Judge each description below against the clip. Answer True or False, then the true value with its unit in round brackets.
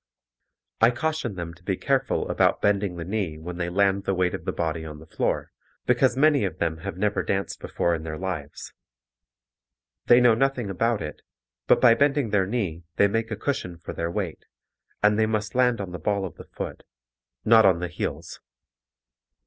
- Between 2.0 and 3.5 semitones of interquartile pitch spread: False (4.8 semitones)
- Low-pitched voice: True (100 Hz)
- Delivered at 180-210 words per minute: True (195 wpm)